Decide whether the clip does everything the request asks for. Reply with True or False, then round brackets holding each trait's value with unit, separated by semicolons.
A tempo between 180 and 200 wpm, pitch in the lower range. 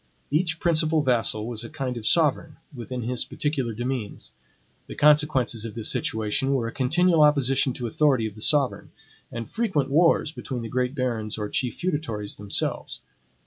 False (165 wpm; 130 Hz)